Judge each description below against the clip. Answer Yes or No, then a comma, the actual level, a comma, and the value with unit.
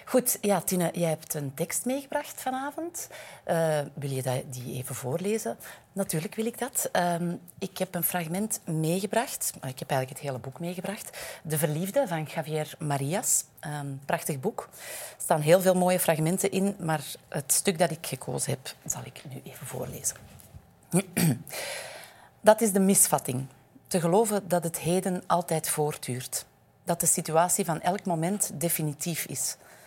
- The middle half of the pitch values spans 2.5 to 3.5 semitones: No, average, 4.6 semitones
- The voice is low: No, medium, 170 Hz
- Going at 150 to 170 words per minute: Yes, average, 160 wpm